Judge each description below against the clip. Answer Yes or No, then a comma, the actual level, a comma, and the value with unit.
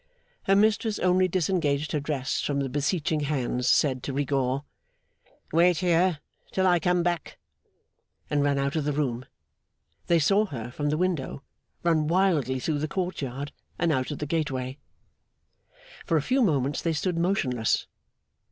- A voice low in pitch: No, medium, 150 Hz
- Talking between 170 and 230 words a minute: No, average, 160 wpm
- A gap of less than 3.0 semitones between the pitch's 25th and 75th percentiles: No, average, 4.2 semitones